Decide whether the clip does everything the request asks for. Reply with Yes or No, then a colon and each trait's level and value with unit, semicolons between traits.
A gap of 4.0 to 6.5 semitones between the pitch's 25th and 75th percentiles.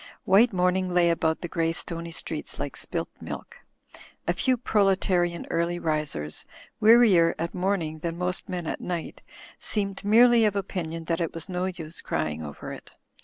No: average, 2.8 semitones